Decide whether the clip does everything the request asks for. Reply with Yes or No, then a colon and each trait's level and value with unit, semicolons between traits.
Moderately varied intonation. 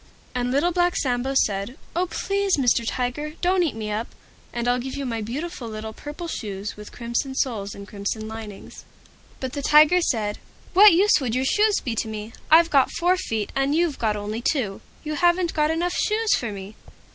No: wide, 7.3 semitones